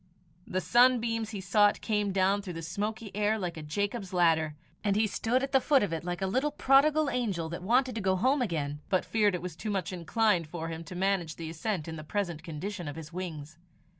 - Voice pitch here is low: No, high, 190 Hz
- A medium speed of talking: No, fast, 225 wpm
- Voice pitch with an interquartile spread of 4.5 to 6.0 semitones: Yes, average, 4.9 semitones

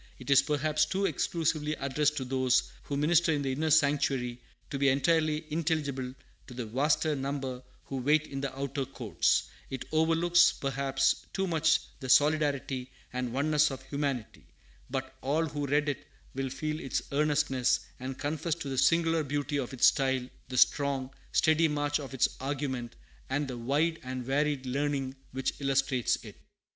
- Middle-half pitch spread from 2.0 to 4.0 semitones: Yes, narrow, 2.4 semitones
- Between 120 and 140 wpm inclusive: No, average, 165 wpm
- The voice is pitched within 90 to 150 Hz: Yes, medium, 140 Hz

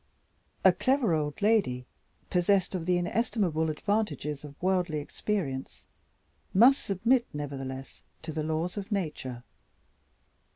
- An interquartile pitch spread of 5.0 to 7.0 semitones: Yes, wide, 5.6 semitones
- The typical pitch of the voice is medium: Yes, medium, 175 Hz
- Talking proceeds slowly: Yes, slow, 115 wpm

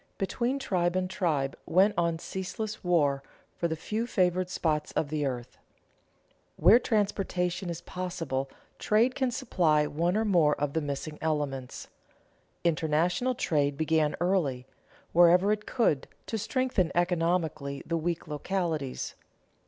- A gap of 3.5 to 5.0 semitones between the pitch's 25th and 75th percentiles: Yes, average, 4.1 semitones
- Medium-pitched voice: Yes, medium, 175 Hz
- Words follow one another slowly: Yes, slow, 130 wpm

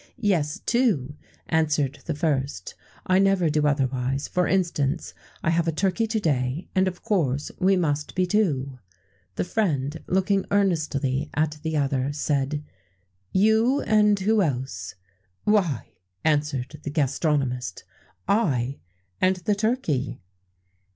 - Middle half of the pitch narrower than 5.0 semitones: No, wide, 5.6 semitones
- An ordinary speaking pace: No, slow, 125 wpm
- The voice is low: No, medium, 155 Hz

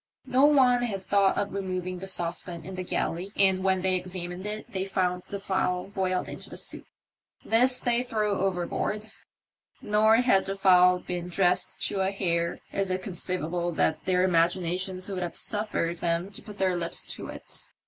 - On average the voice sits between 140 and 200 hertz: Yes, medium, 185 Hz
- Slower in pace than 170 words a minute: No, average, 175 wpm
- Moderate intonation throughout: No, narrow, 2.0 semitones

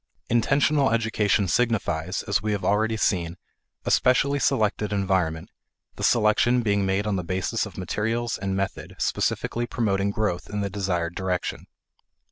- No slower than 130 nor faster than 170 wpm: Yes, average, 145 wpm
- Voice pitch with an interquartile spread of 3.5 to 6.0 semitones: No, average, 3.0 semitones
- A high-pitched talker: No, low, 105 Hz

